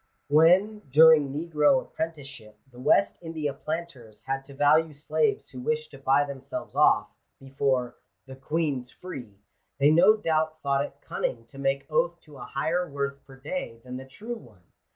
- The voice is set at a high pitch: No, medium, 145 Hz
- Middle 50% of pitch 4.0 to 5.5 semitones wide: No, average, 3.4 semitones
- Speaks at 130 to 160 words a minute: No, average, 175 wpm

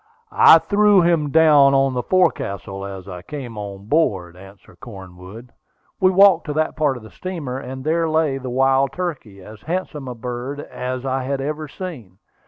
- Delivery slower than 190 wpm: Yes, average, 180 wpm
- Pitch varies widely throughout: Yes, wide, 6.6 semitones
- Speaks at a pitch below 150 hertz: Yes, low, 135 Hz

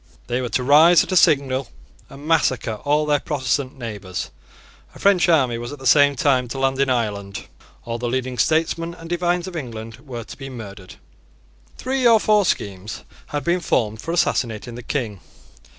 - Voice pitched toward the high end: No, low, 135 Hz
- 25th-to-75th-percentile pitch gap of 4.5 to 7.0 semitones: Yes, wide, 5.4 semitones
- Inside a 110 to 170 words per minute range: No, average, 180 wpm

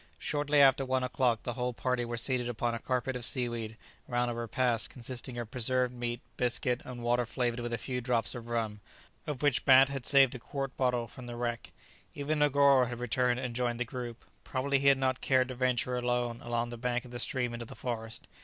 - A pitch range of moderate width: No, narrow, 1.4 semitones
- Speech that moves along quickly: Yes, fast, 220 wpm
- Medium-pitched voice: No, low, 125 Hz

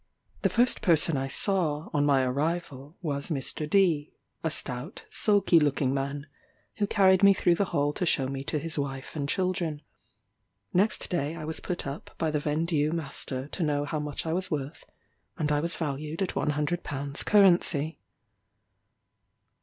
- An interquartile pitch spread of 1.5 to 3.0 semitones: No, average, 3.4 semitones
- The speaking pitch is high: No, medium, 150 Hz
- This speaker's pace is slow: No, average, 170 wpm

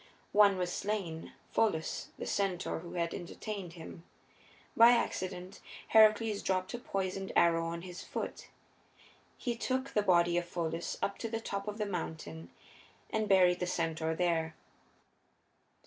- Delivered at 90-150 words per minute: Yes, average, 145 wpm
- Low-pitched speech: No, medium, 185 Hz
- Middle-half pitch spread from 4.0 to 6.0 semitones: No, average, 3.6 semitones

